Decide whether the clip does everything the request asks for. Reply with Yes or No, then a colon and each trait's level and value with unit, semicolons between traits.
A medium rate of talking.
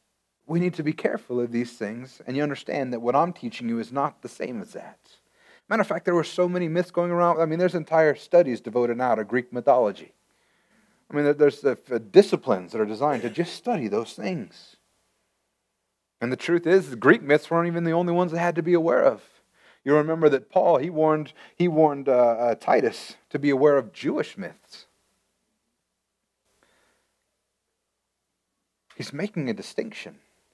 Yes: average, 185 wpm